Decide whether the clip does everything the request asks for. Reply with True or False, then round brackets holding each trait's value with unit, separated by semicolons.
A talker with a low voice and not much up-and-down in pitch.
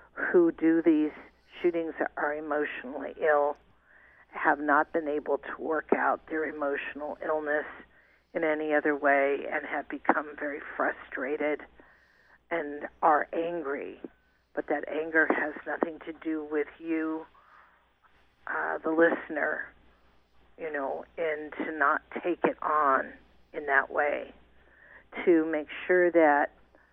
False (155 Hz; 2.0 semitones)